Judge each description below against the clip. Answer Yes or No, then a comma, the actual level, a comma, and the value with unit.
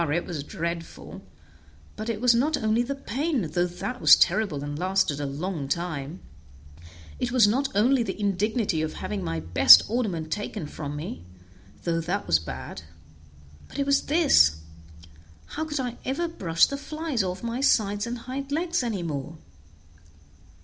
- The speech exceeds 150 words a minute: Yes, average, 165 wpm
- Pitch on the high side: Yes, high, 205 Hz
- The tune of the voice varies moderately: No, wide, 8.1 semitones